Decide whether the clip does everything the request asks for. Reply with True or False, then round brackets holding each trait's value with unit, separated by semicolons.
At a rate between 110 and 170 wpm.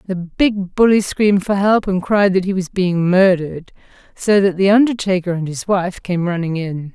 False (200 wpm)